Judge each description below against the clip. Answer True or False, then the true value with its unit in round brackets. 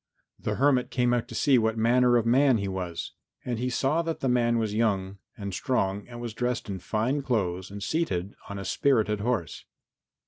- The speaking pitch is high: False (115 Hz)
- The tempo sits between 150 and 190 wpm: False (200 wpm)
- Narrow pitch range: False (3.9 semitones)